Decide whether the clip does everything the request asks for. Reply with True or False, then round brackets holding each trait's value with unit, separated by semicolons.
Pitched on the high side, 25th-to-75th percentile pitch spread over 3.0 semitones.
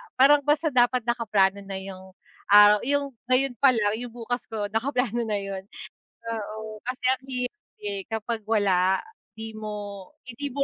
True (225 Hz; 3.7 semitones)